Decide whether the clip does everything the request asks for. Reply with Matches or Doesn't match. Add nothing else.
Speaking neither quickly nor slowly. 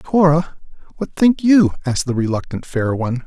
Matches